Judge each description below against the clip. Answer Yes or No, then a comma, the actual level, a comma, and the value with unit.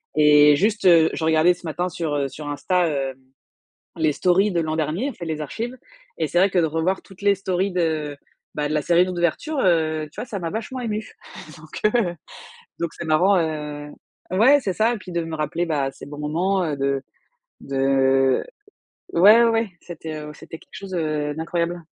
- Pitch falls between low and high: Yes, medium, 165 Hz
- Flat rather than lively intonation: No, average, 3.9 semitones